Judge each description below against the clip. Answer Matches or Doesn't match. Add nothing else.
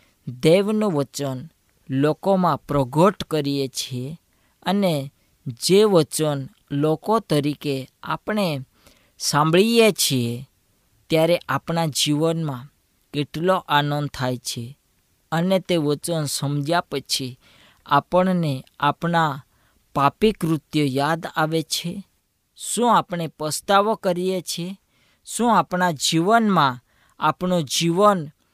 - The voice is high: Doesn't match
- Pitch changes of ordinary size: Matches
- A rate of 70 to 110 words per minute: Matches